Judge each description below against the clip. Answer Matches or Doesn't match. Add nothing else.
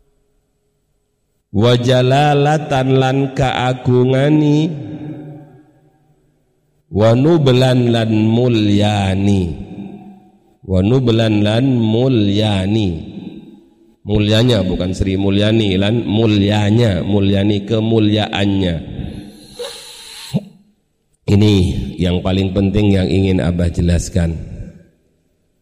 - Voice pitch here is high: Doesn't match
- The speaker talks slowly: Matches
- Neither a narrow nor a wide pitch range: Doesn't match